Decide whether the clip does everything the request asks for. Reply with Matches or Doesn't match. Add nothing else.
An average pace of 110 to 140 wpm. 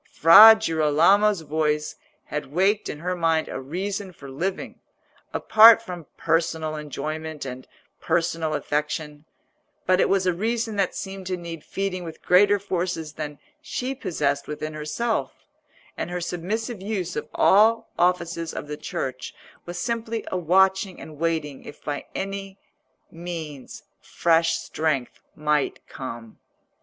Matches